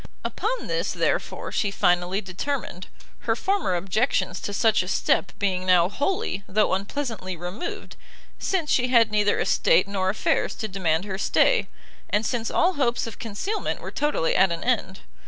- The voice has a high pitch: Yes, high, 205 Hz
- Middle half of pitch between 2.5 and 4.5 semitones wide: No, average, 5.2 semitones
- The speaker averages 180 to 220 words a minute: No, average, 160 wpm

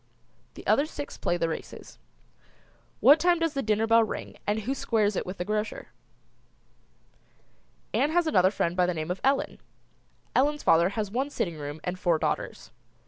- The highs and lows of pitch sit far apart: Yes, wide, 7.4 semitones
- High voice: Yes, high, 210 Hz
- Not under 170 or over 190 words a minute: Yes, average, 175 wpm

